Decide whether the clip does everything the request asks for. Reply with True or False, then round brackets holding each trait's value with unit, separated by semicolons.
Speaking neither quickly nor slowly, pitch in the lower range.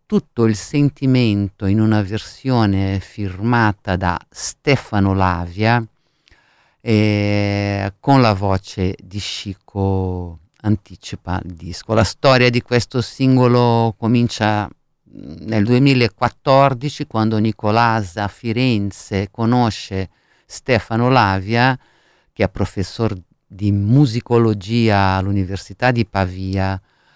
False (90 wpm; 105 Hz)